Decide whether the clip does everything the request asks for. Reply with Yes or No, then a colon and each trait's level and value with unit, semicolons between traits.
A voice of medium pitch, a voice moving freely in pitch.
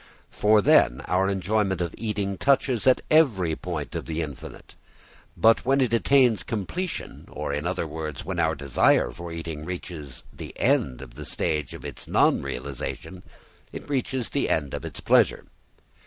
No: very low, 90 Hz; wide, 6.5 semitones